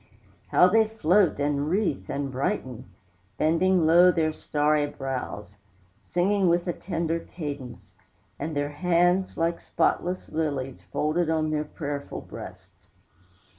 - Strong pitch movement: No, average, 3.6 semitones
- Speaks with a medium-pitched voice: Yes, medium, 160 Hz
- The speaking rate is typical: No, slow, 125 wpm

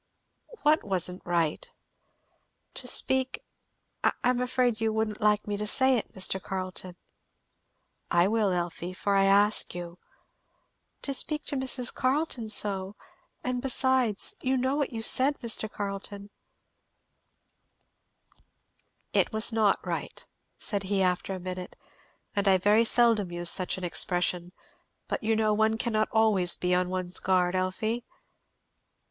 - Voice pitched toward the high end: Yes, high, 205 Hz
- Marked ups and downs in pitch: No, average, 4.1 semitones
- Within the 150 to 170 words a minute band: No, average, 140 wpm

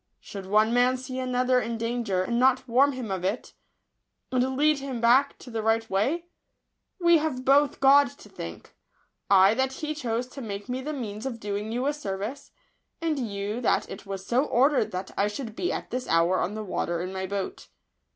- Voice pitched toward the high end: Yes, high, 240 Hz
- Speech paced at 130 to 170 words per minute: No, fast, 205 wpm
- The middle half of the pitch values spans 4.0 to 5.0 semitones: Yes, average, 4.6 semitones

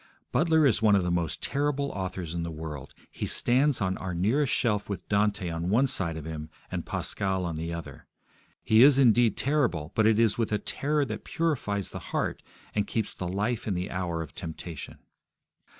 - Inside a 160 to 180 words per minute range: No, average, 200 wpm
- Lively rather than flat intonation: Yes, wide, 5.9 semitones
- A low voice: Yes, low, 100 Hz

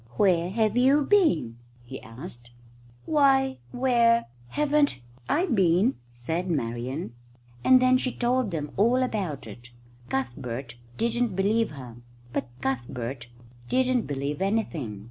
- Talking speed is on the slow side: Yes, slow, 120 wpm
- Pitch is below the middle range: No, high, 190 Hz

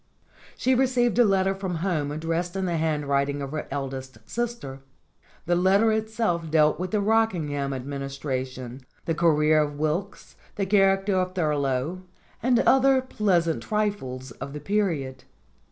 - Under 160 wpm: Yes, average, 145 wpm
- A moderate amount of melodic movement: No, wide, 6.1 semitones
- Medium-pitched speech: Yes, medium, 170 Hz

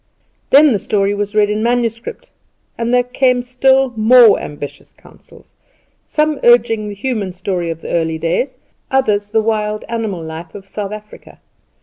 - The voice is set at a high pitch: Yes, high, 215 Hz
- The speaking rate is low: No, average, 160 wpm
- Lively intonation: No, average, 3.8 semitones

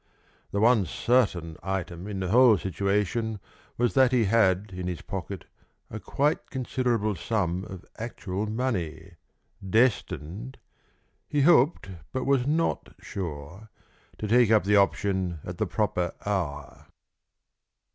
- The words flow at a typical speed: No, slow, 125 wpm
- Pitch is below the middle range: Yes, low, 105 Hz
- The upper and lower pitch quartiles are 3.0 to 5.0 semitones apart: Yes, average, 4.7 semitones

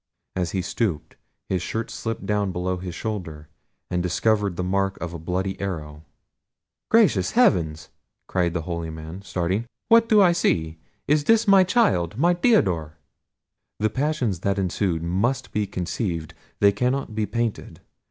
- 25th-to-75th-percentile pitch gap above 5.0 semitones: Yes, wide, 5.5 semitones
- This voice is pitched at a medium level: No, very low, 95 Hz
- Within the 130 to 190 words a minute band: Yes, average, 150 wpm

